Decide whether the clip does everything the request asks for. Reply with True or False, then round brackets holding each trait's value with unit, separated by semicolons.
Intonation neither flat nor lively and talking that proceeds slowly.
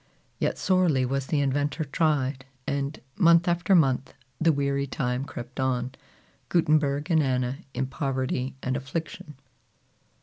True (3.2 semitones; 130 wpm)